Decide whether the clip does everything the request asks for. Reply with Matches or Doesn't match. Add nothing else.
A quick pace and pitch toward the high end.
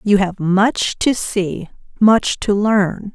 Doesn't match